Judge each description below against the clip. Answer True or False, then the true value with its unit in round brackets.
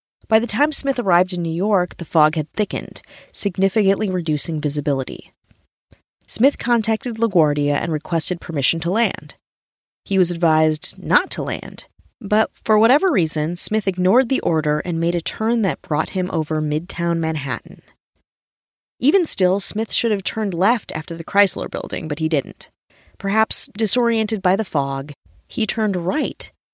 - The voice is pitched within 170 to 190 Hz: True (185 Hz)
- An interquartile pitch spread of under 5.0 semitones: False (5.5 semitones)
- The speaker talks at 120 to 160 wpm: True (155 wpm)